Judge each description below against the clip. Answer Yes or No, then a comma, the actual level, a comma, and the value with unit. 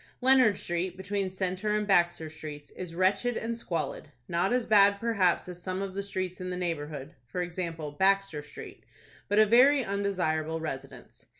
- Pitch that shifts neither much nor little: Yes, average, 3.5 semitones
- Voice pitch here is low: No, medium, 185 Hz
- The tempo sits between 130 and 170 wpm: Yes, average, 160 wpm